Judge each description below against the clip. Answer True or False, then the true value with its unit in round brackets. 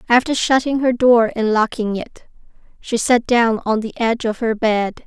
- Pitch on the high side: True (230 Hz)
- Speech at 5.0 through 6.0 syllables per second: False (4.7 syllables/s)